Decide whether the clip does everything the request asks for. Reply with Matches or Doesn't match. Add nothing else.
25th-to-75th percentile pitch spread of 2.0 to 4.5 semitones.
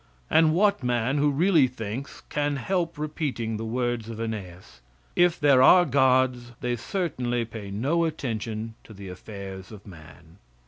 Doesn't match